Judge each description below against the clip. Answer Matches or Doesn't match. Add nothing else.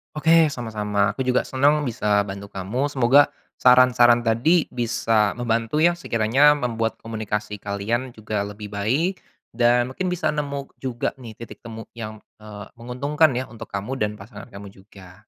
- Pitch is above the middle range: Doesn't match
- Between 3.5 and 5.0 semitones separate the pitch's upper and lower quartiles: Matches